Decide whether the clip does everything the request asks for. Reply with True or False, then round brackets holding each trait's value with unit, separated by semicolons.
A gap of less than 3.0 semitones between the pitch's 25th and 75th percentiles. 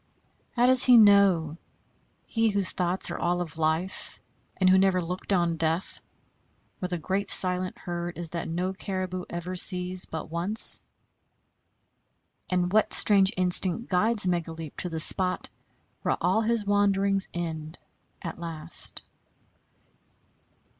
True (2.4 semitones)